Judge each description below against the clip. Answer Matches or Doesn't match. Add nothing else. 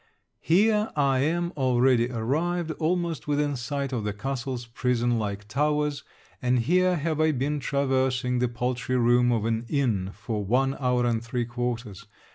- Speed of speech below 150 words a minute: Doesn't match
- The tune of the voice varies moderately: Matches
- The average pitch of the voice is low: Matches